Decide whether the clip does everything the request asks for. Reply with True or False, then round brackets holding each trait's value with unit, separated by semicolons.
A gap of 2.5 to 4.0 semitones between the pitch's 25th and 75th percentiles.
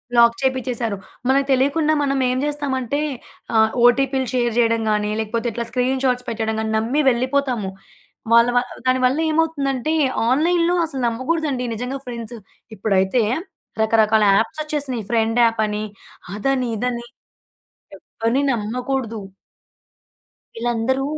True (3.1 semitones)